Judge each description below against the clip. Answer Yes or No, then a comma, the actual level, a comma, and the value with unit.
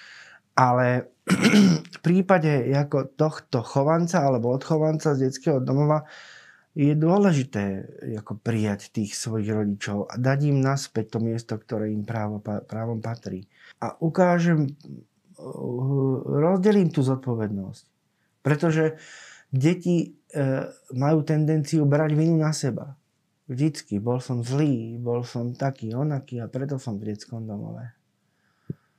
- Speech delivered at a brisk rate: No, average, 115 wpm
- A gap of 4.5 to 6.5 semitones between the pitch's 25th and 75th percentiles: Yes, average, 5.1 semitones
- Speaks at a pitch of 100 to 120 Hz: No, low, 135 Hz